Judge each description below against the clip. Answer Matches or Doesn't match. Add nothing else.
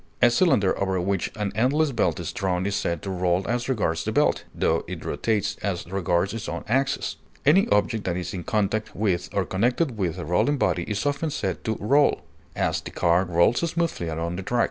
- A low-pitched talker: Matches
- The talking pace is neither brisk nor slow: Doesn't match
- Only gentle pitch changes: Doesn't match